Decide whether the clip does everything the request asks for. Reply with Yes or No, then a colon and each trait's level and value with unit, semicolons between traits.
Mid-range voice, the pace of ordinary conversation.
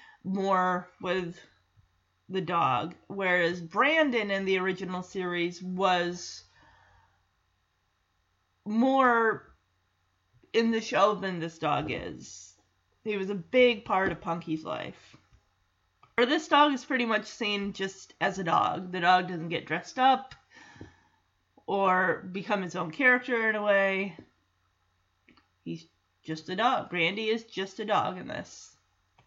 No: medium, 180 Hz; slow, 130 wpm